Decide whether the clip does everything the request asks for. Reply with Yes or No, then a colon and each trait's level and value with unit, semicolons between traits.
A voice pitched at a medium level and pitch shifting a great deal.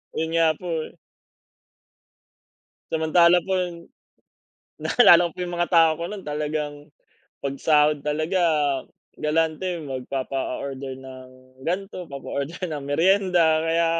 No: medium, 160 Hz; average, 3.7 semitones